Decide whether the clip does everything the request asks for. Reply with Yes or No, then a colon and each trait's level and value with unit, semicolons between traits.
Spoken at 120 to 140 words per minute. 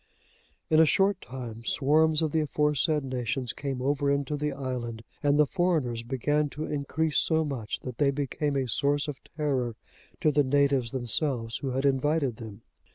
No: average, 170 wpm